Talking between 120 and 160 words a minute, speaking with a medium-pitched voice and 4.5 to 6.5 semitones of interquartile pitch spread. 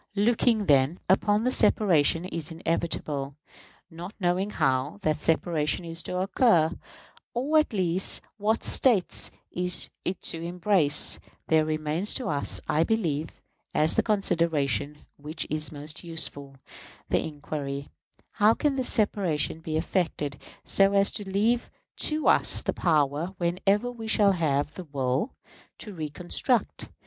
Yes: slow, 135 wpm; medium, 170 Hz; average, 5.1 semitones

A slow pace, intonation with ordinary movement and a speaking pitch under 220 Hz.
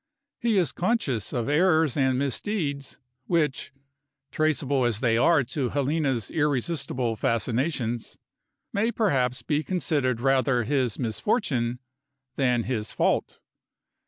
Yes: slow, 110 wpm; average, 4.5 semitones; low, 135 Hz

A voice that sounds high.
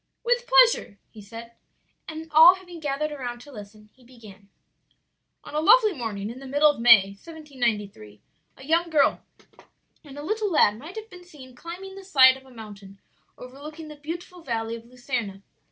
Yes: very high, 275 Hz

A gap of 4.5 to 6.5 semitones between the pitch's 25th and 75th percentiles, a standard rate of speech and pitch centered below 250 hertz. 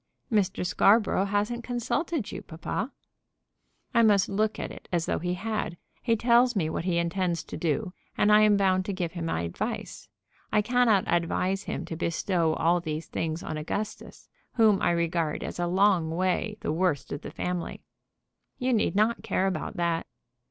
No: average, 3.9 semitones; average, 180 wpm; medium, 185 Hz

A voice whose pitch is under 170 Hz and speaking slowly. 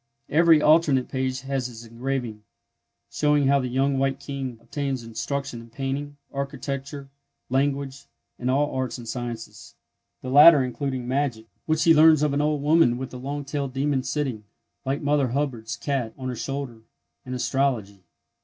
No: low, 135 Hz; average, 155 wpm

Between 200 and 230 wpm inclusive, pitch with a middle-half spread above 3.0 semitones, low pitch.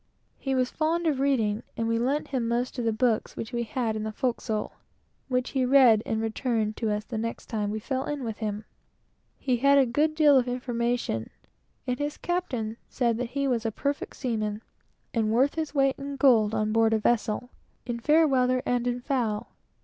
No: fast, 205 wpm; average, 3.4 semitones; high, 245 Hz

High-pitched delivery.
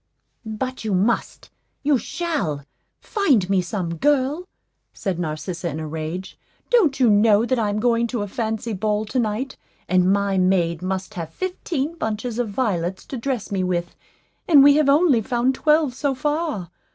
Yes: high, 220 Hz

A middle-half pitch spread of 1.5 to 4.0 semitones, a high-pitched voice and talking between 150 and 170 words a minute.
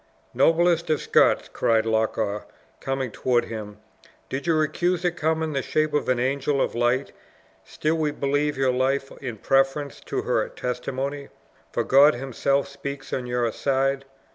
No: average, 2.8 semitones; low, 135 Hz; average, 160 wpm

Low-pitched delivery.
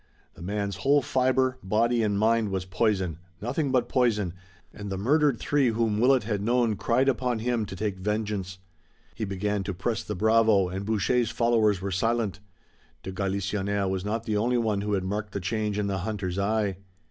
Yes: low, 105 Hz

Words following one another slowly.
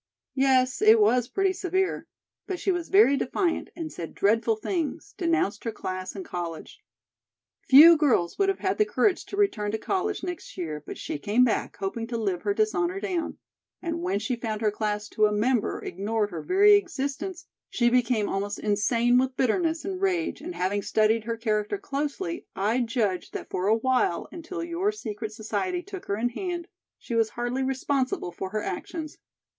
No: average, 185 wpm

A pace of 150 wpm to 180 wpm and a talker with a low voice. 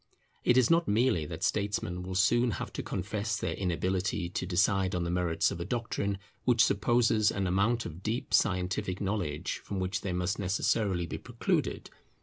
Yes: average, 175 wpm; low, 100 Hz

